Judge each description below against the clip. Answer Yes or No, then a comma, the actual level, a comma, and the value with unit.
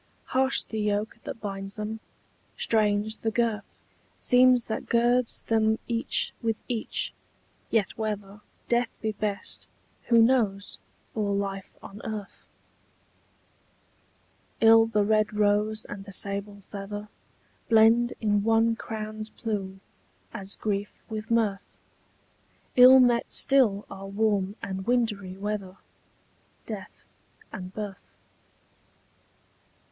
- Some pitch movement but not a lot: No, narrow, 2.1 semitones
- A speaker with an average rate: No, slow, 110 wpm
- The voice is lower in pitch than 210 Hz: No, high, 215 Hz